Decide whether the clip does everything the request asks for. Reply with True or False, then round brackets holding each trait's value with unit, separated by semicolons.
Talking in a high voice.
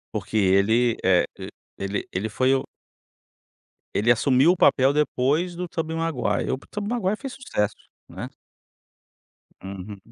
False (130 Hz)